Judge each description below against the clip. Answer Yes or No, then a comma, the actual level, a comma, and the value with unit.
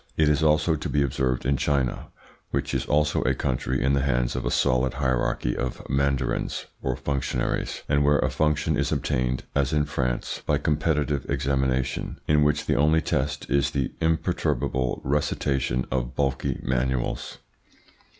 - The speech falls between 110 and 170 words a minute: Yes, average, 160 wpm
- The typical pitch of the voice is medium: No, very low, 70 Hz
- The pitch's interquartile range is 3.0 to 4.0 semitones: No, narrow, 2.6 semitones